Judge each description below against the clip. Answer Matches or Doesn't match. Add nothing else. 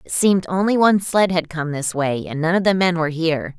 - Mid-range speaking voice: Matches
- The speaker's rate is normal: Doesn't match